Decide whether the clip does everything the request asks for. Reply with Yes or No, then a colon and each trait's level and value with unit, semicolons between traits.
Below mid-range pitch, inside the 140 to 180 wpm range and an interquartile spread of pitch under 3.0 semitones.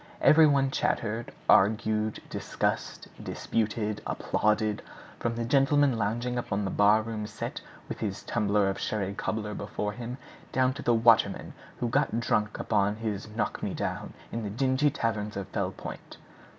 Yes: low, 110 Hz; average, 150 wpm; narrow, 2.4 semitones